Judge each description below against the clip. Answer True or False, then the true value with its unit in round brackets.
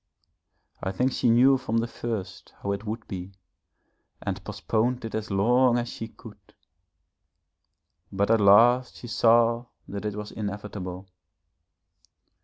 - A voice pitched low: True (110 Hz)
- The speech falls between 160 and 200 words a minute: False (135 wpm)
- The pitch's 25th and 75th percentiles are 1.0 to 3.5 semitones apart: True (2.9 semitones)